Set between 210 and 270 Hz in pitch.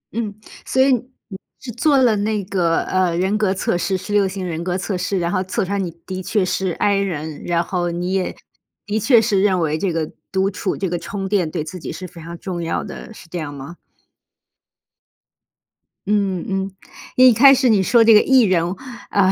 No: high, 190 Hz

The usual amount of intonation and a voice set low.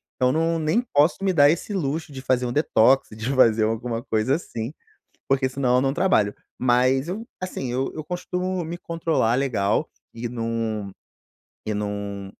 No: wide, 5.9 semitones; low, 130 Hz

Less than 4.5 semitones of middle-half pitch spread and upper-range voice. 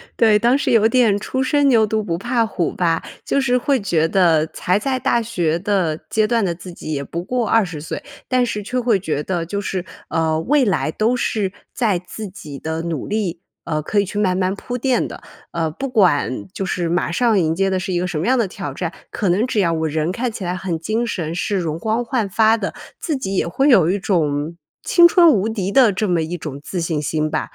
No: average, 5.3 semitones; high, 195 Hz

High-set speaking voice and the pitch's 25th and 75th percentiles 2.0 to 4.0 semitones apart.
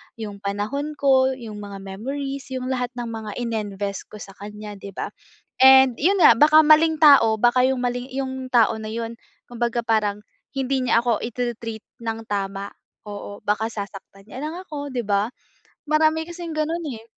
No: high, 235 Hz; average, 4.5 semitones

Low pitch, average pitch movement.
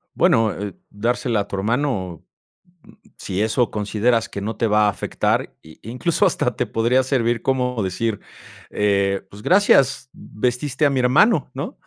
Yes: low, 115 Hz; average, 3.6 semitones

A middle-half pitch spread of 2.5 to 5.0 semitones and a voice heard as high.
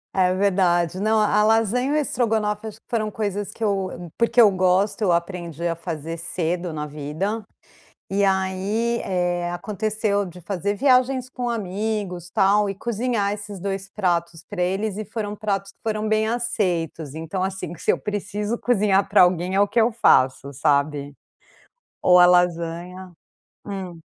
Yes: average, 3.4 semitones; high, 195 Hz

